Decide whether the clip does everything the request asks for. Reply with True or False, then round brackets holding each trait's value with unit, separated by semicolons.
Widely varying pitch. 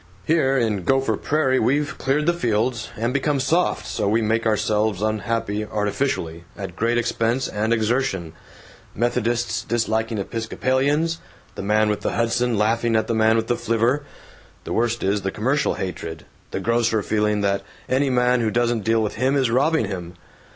False (3.2 semitones)